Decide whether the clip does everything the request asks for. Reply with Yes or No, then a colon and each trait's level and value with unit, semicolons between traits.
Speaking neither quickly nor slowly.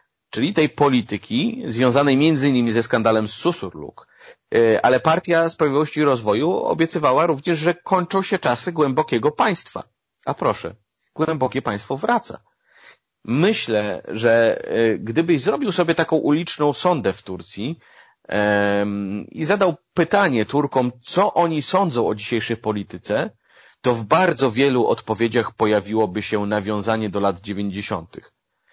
Yes: average, 120 wpm